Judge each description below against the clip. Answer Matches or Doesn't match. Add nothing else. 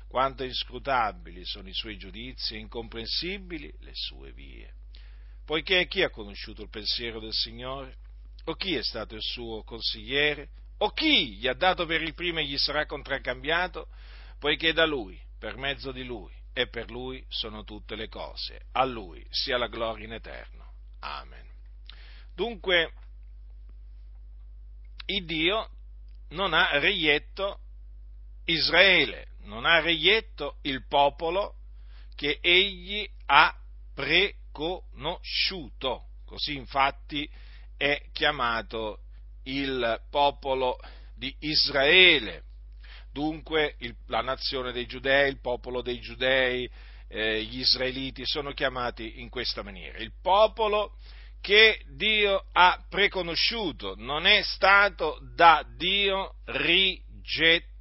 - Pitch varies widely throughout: Matches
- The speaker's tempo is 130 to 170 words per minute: Doesn't match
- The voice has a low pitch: Matches